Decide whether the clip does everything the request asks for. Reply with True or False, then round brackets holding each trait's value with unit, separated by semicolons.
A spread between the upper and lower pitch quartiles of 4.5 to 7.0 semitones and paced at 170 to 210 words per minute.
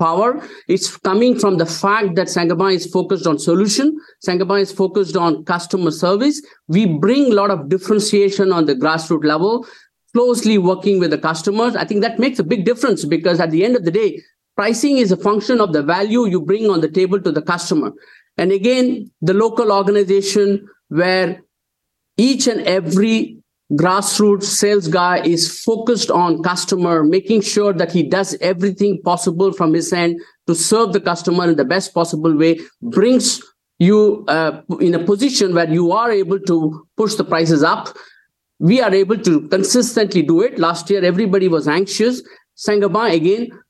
False (3.4 semitones; 175 wpm)